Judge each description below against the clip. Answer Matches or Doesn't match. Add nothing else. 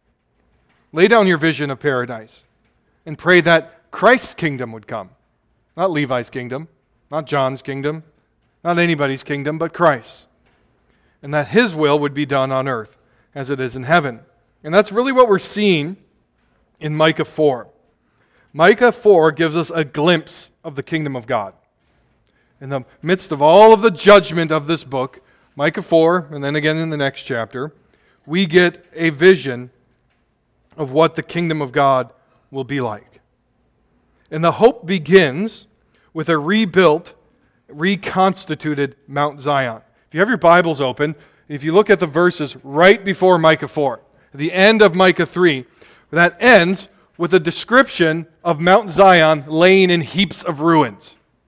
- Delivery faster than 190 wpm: Doesn't match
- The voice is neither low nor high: Matches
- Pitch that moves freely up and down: Doesn't match